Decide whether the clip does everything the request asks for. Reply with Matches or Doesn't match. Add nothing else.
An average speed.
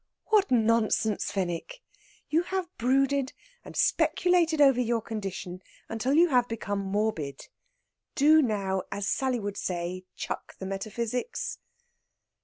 Doesn't match